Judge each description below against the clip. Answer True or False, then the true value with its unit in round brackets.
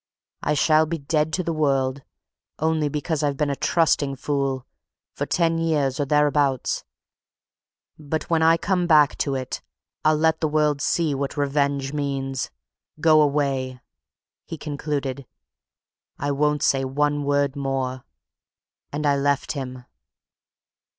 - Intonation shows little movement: True (2.1 semitones)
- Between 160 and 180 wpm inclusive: False (135 wpm)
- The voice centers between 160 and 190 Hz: False (145 Hz)